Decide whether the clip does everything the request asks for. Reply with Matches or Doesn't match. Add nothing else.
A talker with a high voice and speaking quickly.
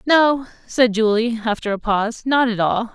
Doesn't match